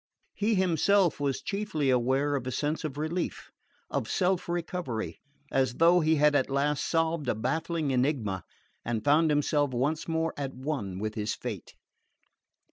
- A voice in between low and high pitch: Yes, medium, 145 Hz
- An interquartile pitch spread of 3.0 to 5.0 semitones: Yes, average, 4.0 semitones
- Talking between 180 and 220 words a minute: No, average, 155 wpm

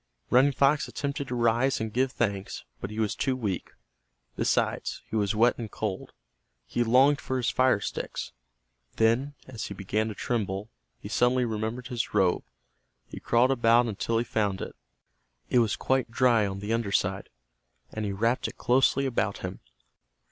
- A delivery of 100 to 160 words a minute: No, average, 170 wpm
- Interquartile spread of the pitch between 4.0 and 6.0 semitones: No, average, 3.3 semitones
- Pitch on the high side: No, low, 115 Hz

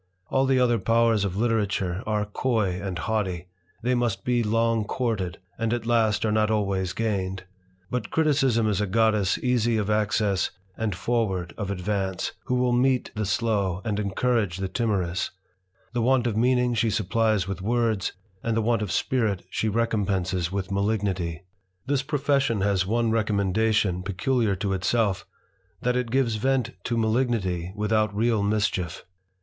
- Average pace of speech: Yes, average, 155 wpm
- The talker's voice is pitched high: No, low, 110 Hz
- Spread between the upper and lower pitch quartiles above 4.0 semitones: No, average, 3.3 semitones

